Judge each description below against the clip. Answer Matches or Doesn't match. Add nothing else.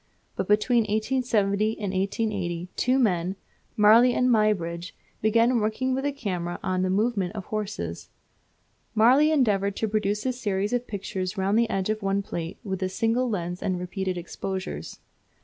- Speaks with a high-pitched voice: Matches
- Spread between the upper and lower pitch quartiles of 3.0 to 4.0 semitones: Matches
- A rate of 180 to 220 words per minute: Doesn't match